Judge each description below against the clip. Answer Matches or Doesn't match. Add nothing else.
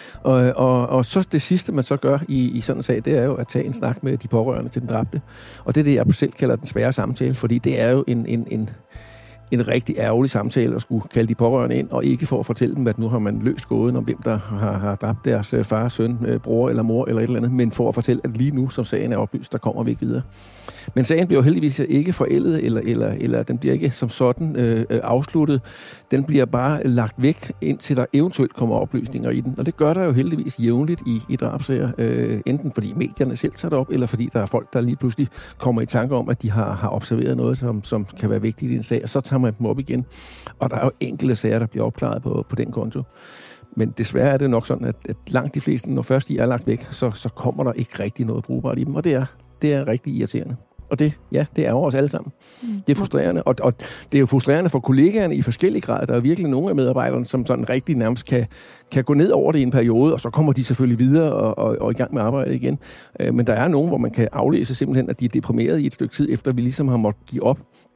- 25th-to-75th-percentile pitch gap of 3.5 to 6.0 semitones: Doesn't match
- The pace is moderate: Doesn't match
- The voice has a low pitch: Matches